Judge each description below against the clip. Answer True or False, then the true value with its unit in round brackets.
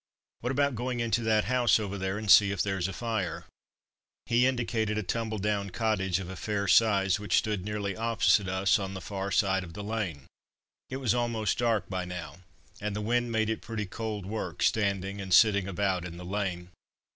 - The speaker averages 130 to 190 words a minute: False (200 wpm)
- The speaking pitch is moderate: False (105 Hz)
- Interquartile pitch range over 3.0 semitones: False (2.7 semitones)